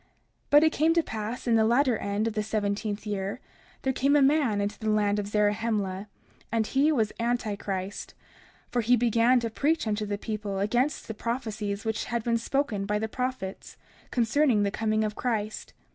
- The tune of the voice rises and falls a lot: No, average, 2.8 semitones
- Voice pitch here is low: No, high, 220 Hz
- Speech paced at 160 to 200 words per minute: Yes, average, 190 wpm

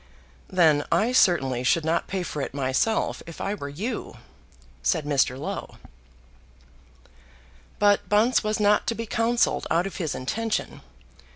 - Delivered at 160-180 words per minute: No, average, 145 wpm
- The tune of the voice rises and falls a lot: Yes, wide, 6.6 semitones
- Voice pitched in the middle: Yes, medium, 180 Hz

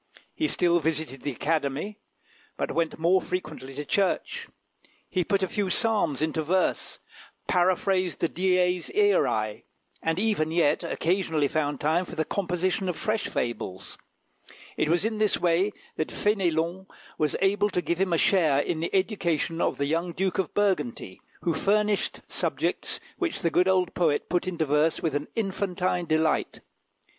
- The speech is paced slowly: No, average, 160 wpm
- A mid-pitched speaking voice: Yes, medium, 175 Hz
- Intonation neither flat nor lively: Yes, average, 3.4 semitones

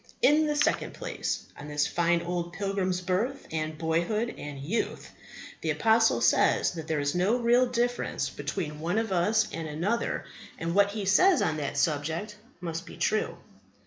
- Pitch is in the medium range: Yes, medium, 180 Hz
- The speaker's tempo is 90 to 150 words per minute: No, average, 170 wpm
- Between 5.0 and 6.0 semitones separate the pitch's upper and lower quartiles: Yes, wide, 5.6 semitones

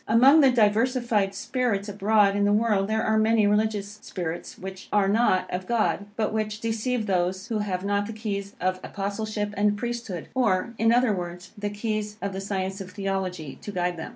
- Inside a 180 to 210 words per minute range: Yes, average, 190 wpm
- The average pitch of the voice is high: Yes, high, 205 Hz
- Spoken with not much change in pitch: Yes, narrow, 2.2 semitones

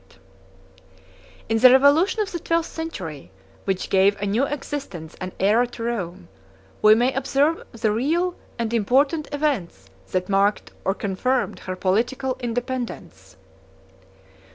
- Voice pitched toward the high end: Yes, high, 235 Hz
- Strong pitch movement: Yes, wide, 6.0 semitones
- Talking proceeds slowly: Yes, slow, 130 wpm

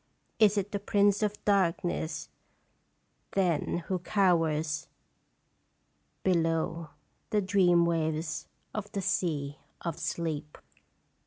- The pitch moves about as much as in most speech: Yes, average, 3.6 semitones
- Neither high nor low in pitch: Yes, medium, 175 Hz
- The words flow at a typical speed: No, slow, 95 wpm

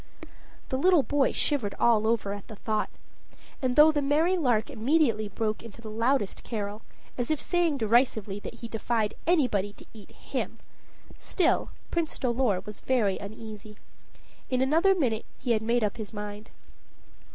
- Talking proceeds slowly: No, average, 160 wpm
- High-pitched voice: Yes, high, 230 Hz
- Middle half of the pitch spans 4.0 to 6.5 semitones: Yes, average, 4.6 semitones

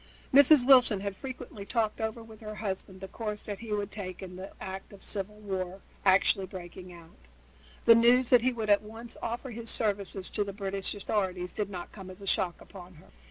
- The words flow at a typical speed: No, fast, 210 wpm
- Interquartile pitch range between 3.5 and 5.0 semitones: No, average, 3.0 semitones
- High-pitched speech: Yes, high, 205 Hz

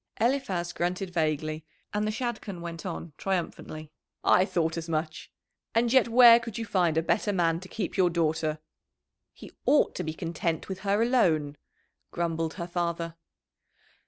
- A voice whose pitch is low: No, medium, 175 Hz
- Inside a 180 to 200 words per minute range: No, average, 160 wpm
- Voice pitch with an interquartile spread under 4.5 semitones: Yes, average, 4.1 semitones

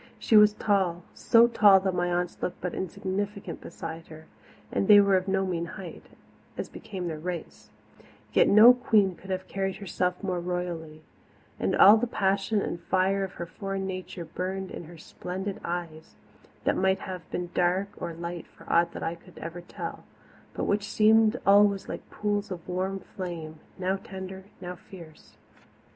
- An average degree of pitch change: No, narrow, 2.2 semitones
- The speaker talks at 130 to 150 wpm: No, average, 175 wpm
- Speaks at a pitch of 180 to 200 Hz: Yes, medium, 185 Hz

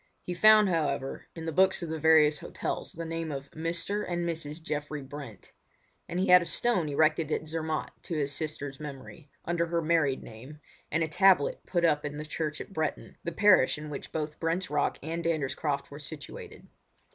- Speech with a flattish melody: Yes, narrow, 2.3 semitones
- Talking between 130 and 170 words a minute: No, average, 195 wpm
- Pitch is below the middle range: No, medium, 160 Hz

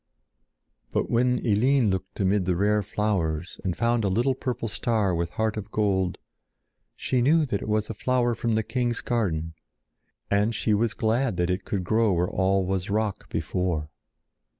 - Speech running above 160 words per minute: Yes, average, 175 wpm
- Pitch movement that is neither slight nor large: Yes, average, 3.7 semitones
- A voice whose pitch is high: No, low, 105 Hz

